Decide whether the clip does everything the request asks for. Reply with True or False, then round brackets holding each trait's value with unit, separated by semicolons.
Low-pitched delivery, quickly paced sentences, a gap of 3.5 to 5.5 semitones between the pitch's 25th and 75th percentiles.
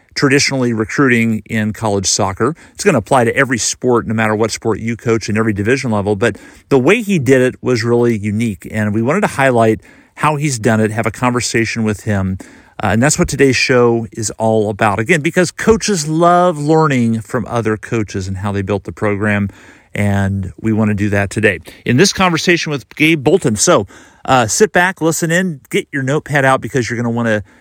True (115 Hz; 210 wpm; 4.8 semitones)